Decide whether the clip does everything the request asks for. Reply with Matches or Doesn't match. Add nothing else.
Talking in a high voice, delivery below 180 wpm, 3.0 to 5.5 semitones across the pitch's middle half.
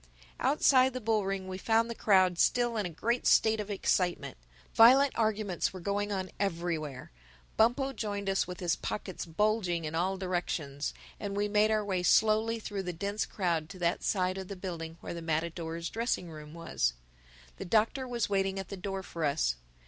Doesn't match